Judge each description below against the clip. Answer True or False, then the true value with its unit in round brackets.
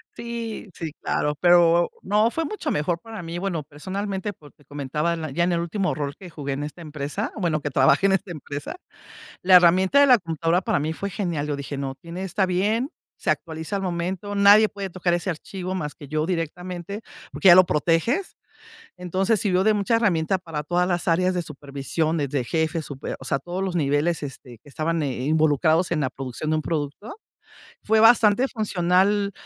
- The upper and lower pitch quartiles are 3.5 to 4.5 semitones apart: True (4.2 semitones)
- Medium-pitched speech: True (175 Hz)